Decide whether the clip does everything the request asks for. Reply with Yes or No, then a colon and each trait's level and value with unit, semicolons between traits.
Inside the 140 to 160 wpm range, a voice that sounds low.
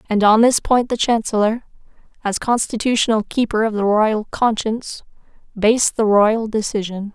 No: average, 145 wpm; high, 220 Hz